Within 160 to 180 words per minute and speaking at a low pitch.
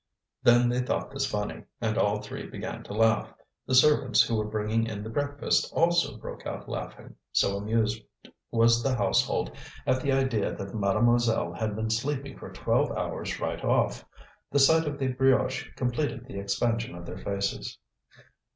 Yes: average, 170 wpm; low, 115 Hz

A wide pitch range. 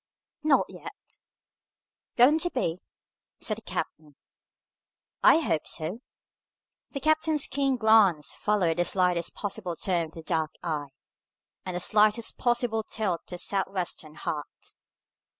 Yes: wide, 6.3 semitones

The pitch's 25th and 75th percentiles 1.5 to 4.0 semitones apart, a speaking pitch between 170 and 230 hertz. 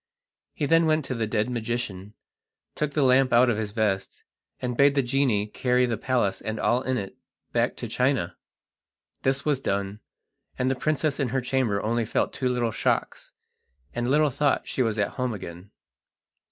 No: average, 3.7 semitones; low, 125 Hz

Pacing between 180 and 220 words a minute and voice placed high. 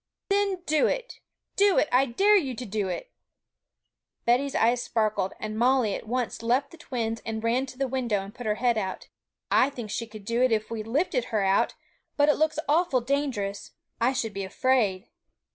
Yes: average, 195 wpm; high, 240 Hz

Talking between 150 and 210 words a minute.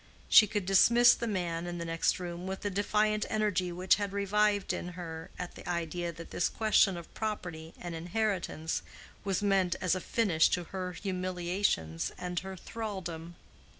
Yes: average, 170 wpm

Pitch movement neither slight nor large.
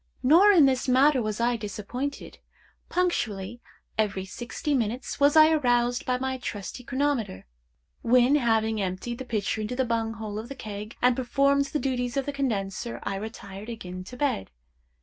Yes: average, 4.1 semitones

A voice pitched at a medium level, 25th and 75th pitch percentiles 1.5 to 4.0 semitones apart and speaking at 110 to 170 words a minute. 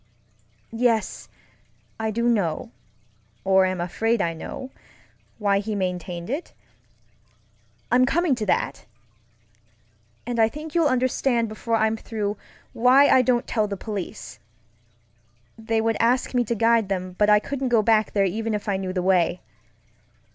No: high, 220 Hz; average, 3.6 semitones; average, 145 wpm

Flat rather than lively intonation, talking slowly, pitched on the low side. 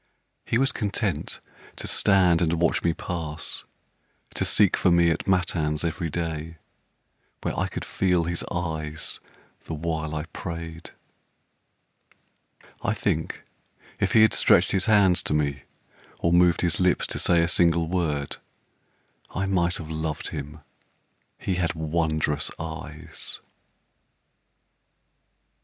Yes: narrow, 2.1 semitones; slow, 130 wpm; very low, 85 Hz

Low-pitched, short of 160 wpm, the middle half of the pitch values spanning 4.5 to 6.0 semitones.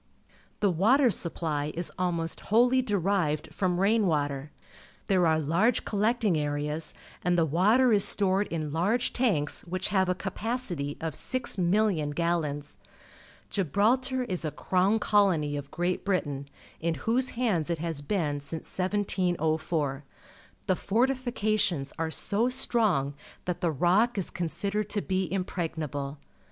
No: medium, 180 Hz; slow, 135 wpm; average, 4.9 semitones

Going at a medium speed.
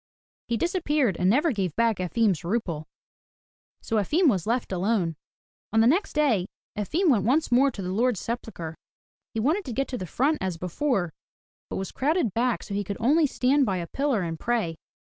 Yes: average, 190 wpm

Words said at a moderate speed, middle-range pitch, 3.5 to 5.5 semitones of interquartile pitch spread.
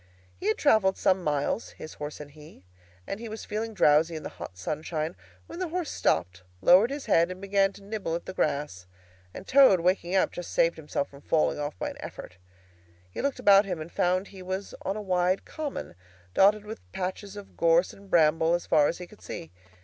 No: fast, 210 wpm; medium, 180 Hz; average, 4.5 semitones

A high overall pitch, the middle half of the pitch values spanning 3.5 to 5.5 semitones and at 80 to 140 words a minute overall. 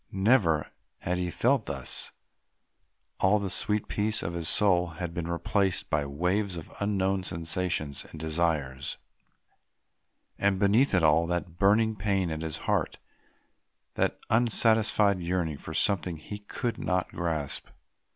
No: very low, 90 Hz; average, 3.9 semitones; slow, 135 wpm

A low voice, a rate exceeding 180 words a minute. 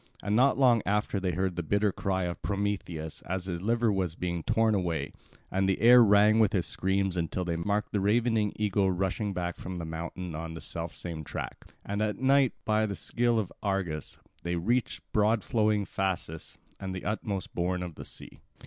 Yes: very low, 95 Hz; average, 195 wpm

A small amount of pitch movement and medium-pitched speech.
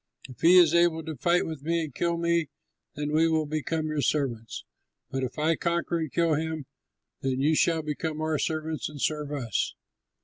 Yes: narrow, 2.0 semitones; medium, 155 Hz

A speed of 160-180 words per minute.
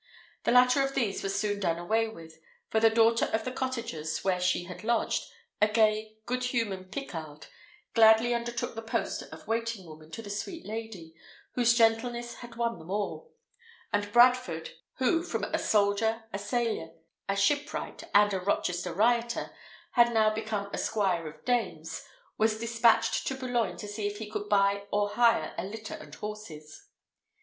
Yes: average, 170 wpm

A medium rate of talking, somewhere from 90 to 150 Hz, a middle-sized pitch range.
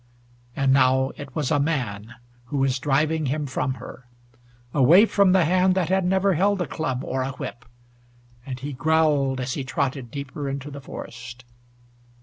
Yes: average, 170 wpm; medium, 140 Hz; average, 3.6 semitones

